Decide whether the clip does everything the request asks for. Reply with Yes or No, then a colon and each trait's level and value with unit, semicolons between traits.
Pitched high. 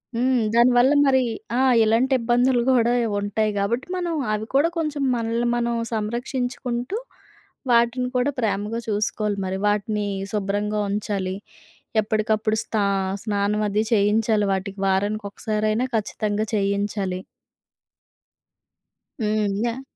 Yes: high, 215 Hz